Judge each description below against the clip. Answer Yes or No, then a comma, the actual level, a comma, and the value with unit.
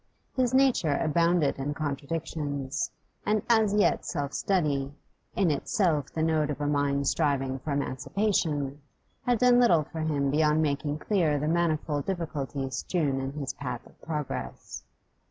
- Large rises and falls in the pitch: No, average, 3.4 semitones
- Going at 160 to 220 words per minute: No, average, 145 wpm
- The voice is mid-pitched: Yes, medium, 150 Hz